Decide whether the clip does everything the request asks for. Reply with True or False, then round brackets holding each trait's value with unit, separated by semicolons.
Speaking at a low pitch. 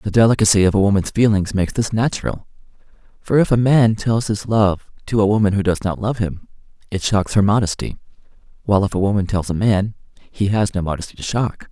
True (105 Hz)